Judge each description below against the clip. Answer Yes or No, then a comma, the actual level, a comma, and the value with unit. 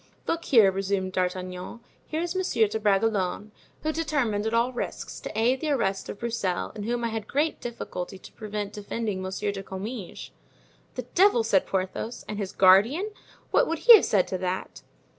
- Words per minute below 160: No, average, 180 wpm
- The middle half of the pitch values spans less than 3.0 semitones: No, average, 4.4 semitones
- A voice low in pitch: No, high, 215 Hz